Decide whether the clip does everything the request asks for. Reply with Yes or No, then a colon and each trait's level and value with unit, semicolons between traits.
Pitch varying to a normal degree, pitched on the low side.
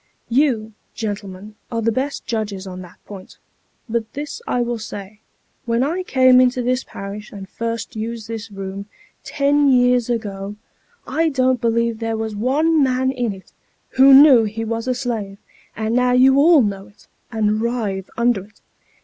No: average, 3.4 semitones; high, 230 Hz